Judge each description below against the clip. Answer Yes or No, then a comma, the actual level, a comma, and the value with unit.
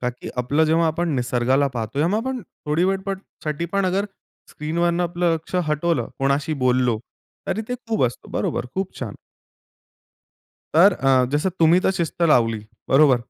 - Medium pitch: Yes, medium, 160 Hz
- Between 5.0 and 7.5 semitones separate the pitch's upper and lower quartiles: Yes, wide, 5.5 semitones